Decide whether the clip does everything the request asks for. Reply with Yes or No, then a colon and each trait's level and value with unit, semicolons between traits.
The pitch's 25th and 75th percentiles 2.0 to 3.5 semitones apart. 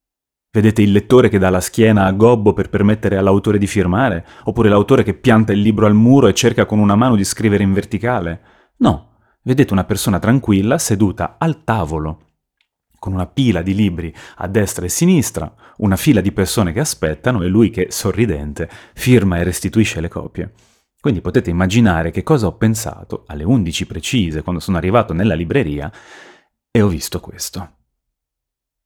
No: average, 4.1 semitones